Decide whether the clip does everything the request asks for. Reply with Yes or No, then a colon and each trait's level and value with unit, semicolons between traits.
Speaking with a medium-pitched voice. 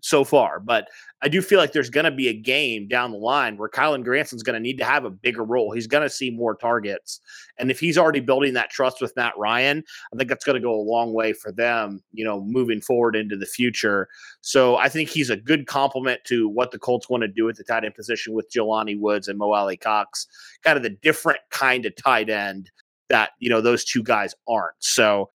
No: low, 120 Hz